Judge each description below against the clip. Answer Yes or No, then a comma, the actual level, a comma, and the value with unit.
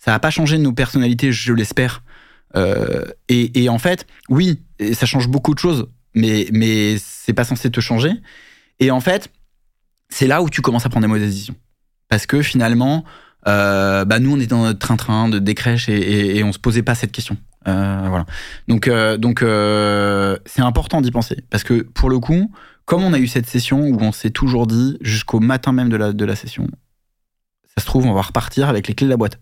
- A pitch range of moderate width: Yes, average, 3.6 semitones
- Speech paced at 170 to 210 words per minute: No, fast, 220 wpm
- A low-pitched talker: Yes, low, 120 Hz